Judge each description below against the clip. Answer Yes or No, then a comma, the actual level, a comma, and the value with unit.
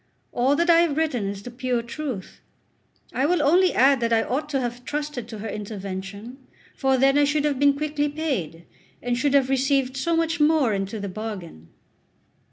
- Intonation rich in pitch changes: No, average, 4.9 semitones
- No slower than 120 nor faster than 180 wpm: No, average, 190 wpm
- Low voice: No, very high, 265 Hz